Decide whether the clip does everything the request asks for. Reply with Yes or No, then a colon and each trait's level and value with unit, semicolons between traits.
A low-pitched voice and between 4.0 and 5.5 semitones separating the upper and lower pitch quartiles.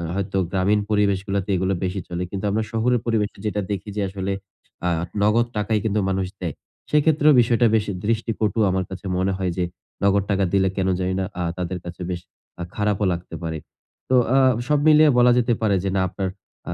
No: low, 100 Hz; average, 2.9 semitones